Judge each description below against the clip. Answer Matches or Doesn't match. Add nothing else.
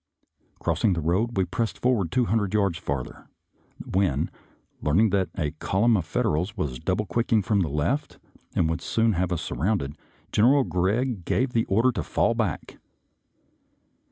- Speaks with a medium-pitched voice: Doesn't match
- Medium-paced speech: Matches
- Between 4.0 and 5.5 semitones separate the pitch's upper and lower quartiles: Matches